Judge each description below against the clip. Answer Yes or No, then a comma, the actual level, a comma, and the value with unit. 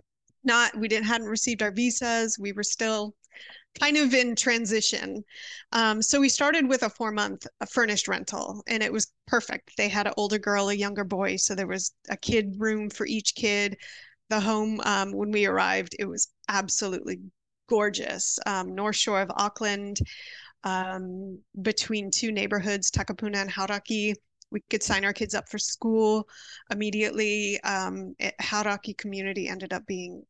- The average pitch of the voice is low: No, high, 210 Hz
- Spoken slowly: No, average, 165 wpm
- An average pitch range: No, narrow, 2.0 semitones